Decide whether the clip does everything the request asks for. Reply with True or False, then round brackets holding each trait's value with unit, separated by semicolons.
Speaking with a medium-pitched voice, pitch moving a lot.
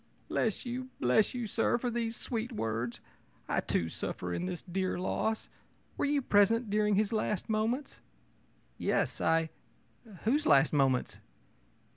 False (215 Hz; 6.3 semitones)